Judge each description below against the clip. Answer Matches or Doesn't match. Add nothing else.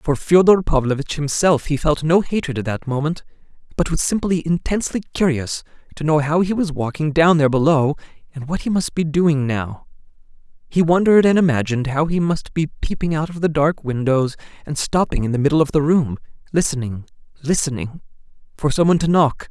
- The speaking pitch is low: Doesn't match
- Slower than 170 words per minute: Doesn't match